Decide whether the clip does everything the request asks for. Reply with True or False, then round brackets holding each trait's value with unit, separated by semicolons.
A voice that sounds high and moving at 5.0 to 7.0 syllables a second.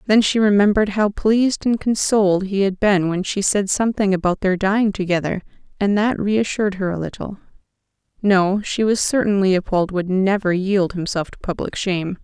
True (200 Hz; 5.3 syllables/s)